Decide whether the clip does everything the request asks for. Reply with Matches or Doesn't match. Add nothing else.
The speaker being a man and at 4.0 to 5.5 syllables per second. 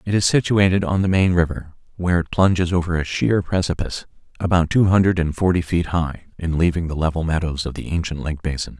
Doesn't match